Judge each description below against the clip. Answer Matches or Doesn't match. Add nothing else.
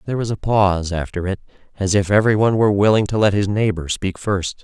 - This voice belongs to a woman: Doesn't match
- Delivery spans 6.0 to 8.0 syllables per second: Matches